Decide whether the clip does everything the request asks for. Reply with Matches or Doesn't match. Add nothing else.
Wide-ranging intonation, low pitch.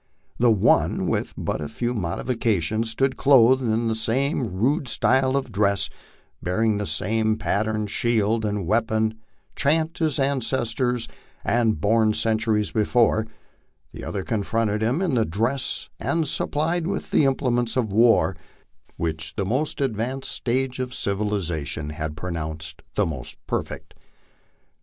Doesn't match